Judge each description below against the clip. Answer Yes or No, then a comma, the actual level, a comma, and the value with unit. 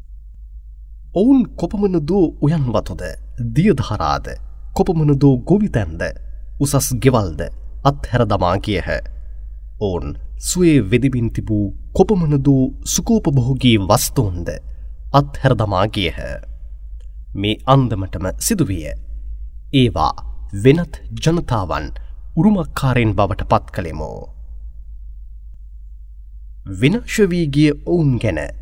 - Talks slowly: Yes, slow, 70 wpm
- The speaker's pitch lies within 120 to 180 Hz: No, low, 105 Hz